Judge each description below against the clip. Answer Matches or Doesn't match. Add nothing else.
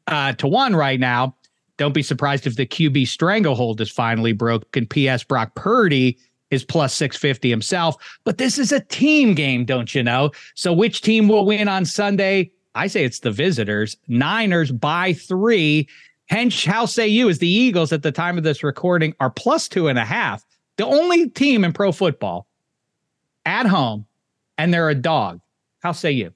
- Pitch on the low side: Doesn't match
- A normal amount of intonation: Doesn't match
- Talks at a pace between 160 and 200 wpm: Matches